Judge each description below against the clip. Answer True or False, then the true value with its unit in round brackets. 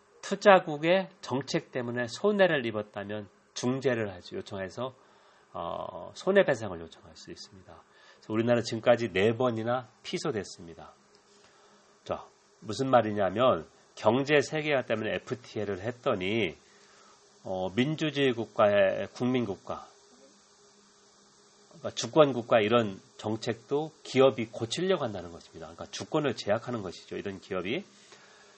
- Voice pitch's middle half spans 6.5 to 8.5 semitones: False (5.5 semitones)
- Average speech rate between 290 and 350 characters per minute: True (295 characters per minute)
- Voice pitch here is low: True (125 Hz)